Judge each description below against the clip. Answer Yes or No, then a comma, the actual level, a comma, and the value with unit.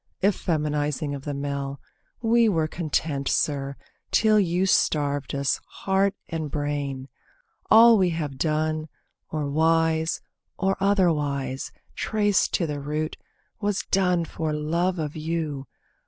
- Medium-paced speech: No, slow, 125 wpm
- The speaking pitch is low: No, medium, 155 Hz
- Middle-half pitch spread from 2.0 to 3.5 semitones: No, average, 4.0 semitones